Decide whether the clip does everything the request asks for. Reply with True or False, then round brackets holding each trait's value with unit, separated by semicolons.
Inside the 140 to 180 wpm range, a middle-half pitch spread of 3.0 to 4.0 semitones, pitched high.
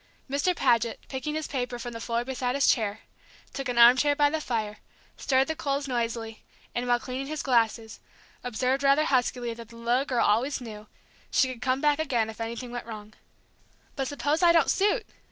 False (195 wpm; 3.3 semitones; 250 Hz)